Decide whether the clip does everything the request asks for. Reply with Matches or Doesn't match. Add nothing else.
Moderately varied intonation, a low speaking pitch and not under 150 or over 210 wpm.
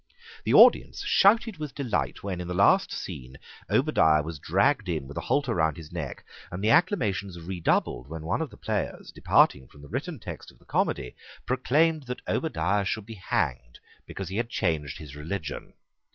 Doesn't match